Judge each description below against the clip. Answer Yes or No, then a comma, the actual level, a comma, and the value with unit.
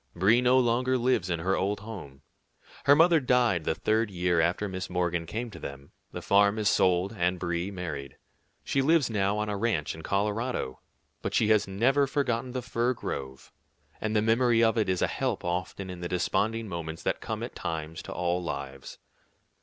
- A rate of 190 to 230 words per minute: Yes, average, 195 wpm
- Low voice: Yes, low, 100 Hz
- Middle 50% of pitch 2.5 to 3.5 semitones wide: No, average, 5.0 semitones